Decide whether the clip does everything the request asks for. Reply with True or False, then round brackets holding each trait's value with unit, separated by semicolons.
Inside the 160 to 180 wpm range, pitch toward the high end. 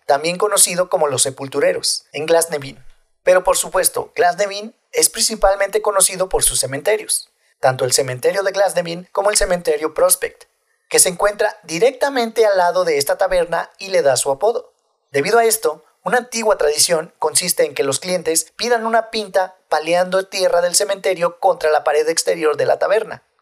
True (165 wpm; 205 Hz)